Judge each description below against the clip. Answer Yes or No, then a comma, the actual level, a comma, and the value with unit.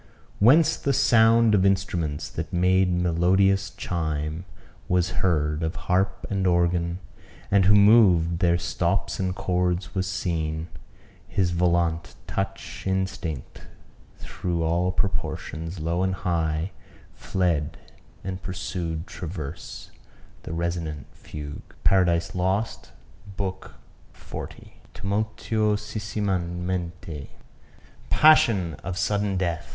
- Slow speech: Yes, slow, 100 wpm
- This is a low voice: Yes, very low, 90 Hz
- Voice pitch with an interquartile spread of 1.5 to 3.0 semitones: Yes, narrow, 2.5 semitones